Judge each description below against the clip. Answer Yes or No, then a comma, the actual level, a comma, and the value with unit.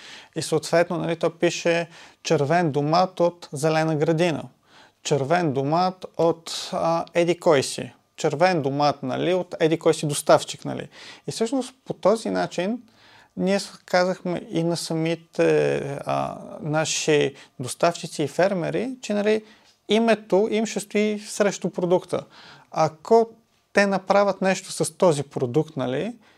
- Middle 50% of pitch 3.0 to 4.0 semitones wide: Yes, average, 3.4 semitones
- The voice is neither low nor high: Yes, medium, 170 Hz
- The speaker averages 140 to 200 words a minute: No, average, 125 wpm